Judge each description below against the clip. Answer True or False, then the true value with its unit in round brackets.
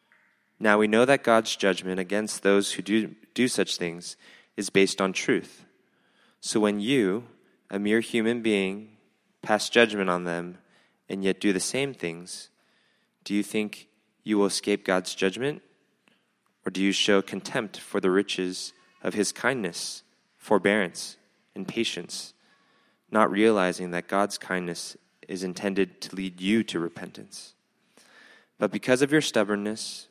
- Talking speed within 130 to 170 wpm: True (145 wpm)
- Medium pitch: False (100 Hz)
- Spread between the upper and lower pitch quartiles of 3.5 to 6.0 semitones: False (2.6 semitones)